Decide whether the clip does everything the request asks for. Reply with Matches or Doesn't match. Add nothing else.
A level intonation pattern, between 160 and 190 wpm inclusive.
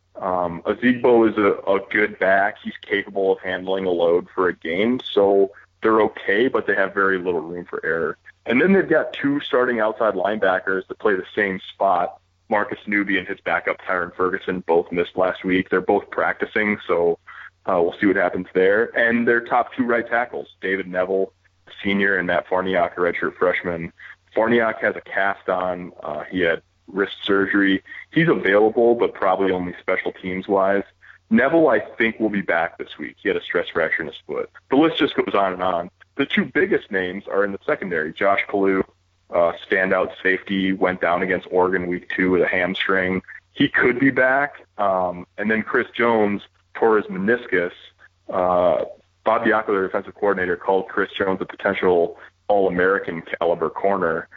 Doesn't match